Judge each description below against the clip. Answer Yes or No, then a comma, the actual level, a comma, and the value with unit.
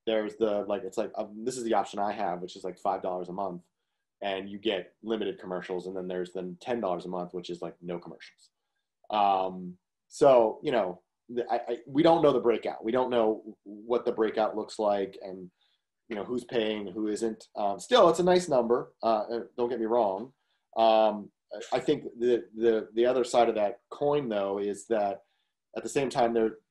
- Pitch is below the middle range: Yes, low, 105 Hz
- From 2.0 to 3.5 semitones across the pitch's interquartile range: No, average, 3.9 semitones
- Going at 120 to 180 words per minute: No, fast, 205 wpm